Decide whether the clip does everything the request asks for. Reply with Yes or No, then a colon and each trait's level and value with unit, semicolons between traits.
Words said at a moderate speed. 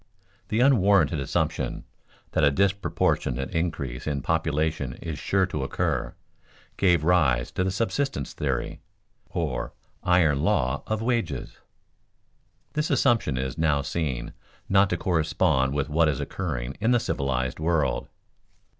No: slow, 130 wpm